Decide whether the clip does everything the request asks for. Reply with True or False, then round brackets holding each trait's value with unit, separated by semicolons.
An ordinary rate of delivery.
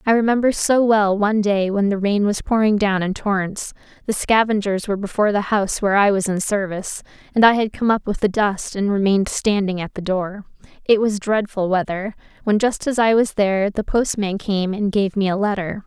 False (210 wpm)